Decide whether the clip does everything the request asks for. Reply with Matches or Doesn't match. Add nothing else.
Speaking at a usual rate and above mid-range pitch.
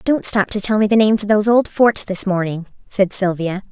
Doesn't match